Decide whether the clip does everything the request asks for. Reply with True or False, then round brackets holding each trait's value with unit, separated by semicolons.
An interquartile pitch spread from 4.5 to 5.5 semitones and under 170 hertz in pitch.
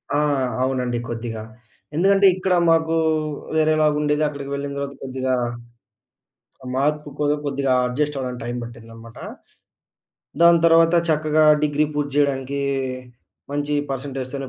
False (2.7 semitones; 140 Hz)